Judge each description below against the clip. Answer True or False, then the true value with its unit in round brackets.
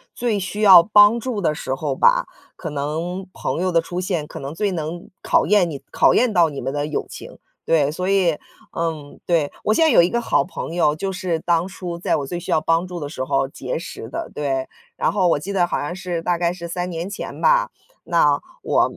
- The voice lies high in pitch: False (170 Hz)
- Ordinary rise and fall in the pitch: True (3.7 semitones)